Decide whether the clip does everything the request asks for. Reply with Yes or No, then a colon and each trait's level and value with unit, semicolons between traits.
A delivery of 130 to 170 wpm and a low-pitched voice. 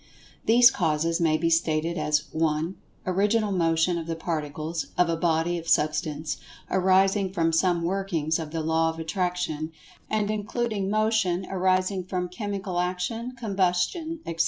No: average, 150 wpm; medium, 175 Hz